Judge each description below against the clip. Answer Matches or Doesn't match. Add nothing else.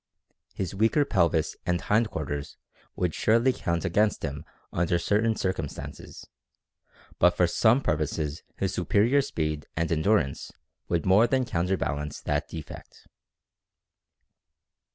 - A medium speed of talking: Doesn't match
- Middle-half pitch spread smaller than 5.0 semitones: Doesn't match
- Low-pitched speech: Matches